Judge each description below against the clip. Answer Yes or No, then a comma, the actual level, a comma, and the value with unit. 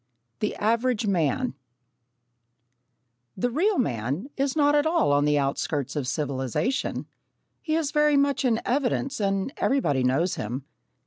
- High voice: Yes, high, 225 Hz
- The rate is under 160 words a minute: Yes, slow, 135 wpm